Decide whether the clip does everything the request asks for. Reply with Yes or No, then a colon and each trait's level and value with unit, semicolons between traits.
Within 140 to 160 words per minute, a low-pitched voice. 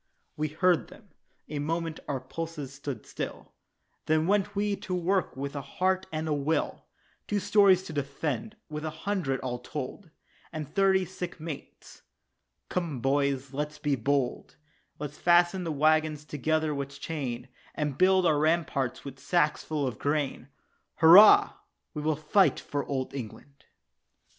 No: average, 155 wpm; medium, 155 Hz